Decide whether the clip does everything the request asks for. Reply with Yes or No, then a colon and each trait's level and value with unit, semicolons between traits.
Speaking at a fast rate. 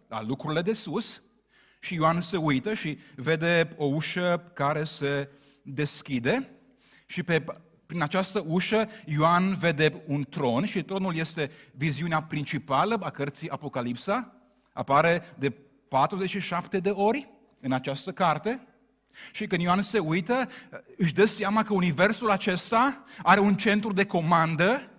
No: average, 135 wpm